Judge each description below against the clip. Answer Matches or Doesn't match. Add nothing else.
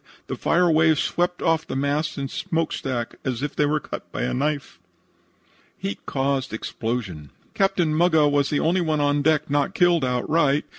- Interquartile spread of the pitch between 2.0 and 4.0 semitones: Matches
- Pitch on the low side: Doesn't match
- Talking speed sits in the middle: Matches